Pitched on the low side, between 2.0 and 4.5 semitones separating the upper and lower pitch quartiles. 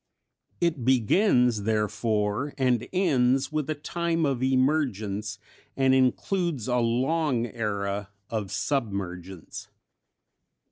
No: low, 125 Hz; average, 5.3 semitones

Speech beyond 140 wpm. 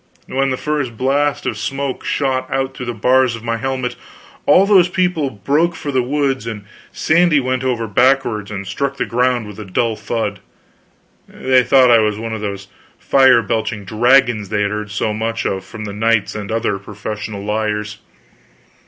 Yes: average, 180 wpm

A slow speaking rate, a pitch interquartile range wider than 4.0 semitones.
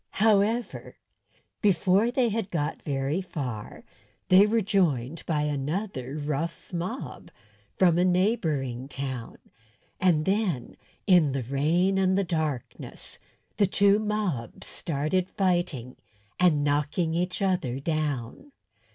Yes: slow, 115 wpm; wide, 5.4 semitones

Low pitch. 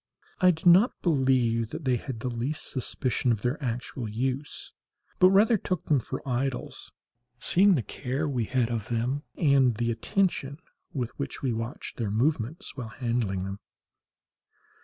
Yes: low, 130 Hz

